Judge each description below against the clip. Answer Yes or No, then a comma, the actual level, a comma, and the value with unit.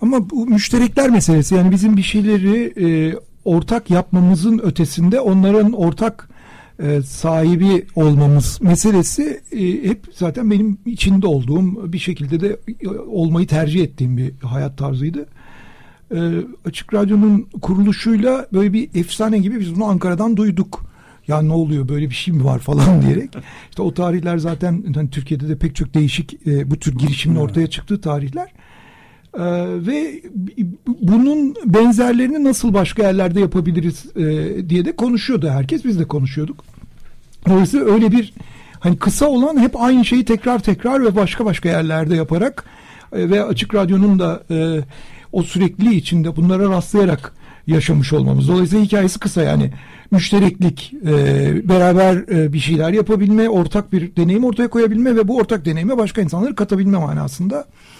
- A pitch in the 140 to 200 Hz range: Yes, medium, 185 Hz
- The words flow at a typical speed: No, fast, 145 wpm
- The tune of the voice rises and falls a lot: No, average, 4.8 semitones